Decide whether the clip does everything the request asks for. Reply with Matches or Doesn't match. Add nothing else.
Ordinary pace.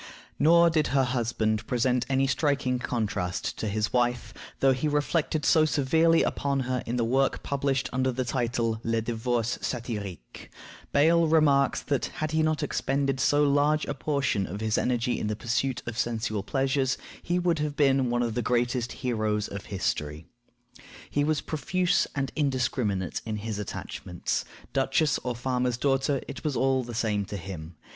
Matches